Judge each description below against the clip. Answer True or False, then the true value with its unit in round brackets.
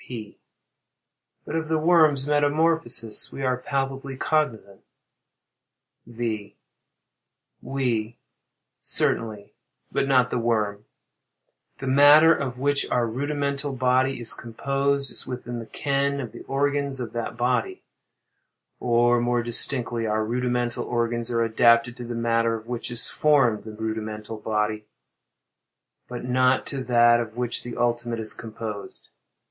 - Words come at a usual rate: False (130 wpm)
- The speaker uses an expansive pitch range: False (3.2 semitones)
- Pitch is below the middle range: True (120 Hz)